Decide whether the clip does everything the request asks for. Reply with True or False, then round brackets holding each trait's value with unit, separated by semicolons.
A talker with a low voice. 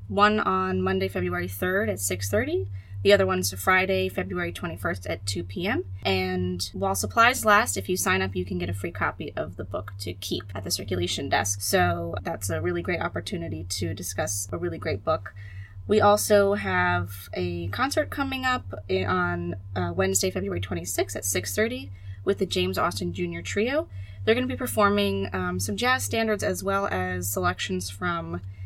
True (95 Hz)